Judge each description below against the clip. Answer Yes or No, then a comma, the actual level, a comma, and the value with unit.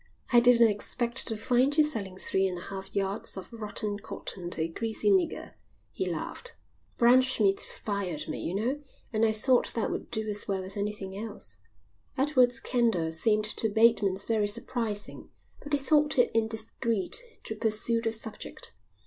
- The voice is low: No, high, 220 Hz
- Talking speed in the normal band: Yes, average, 165 wpm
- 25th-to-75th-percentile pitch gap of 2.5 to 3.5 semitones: Yes, average, 3.1 semitones